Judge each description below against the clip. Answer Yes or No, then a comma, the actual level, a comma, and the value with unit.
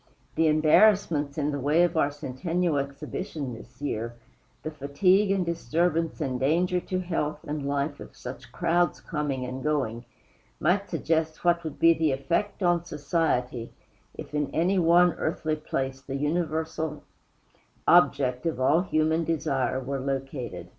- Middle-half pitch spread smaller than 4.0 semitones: Yes, average, 3.5 semitones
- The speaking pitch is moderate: Yes, medium, 155 Hz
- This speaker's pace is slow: No, average, 150 wpm